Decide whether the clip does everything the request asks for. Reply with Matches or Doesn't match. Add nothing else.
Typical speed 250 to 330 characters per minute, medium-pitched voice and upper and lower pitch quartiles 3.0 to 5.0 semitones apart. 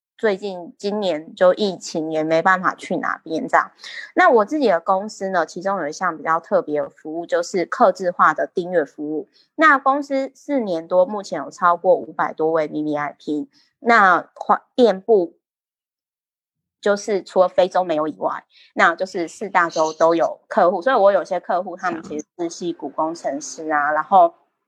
Matches